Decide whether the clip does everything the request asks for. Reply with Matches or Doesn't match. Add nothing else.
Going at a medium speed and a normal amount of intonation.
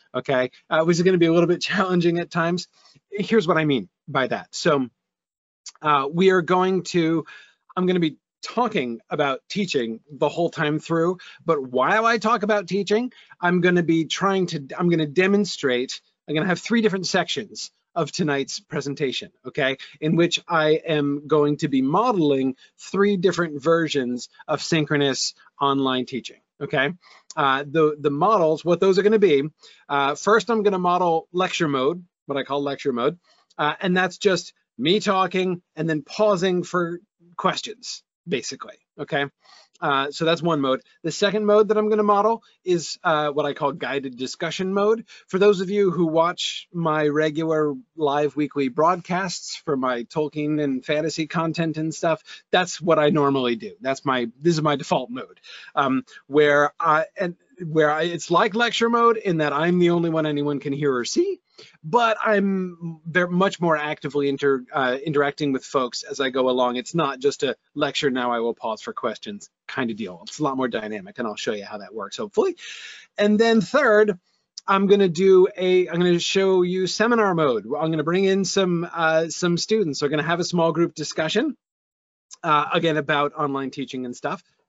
Matches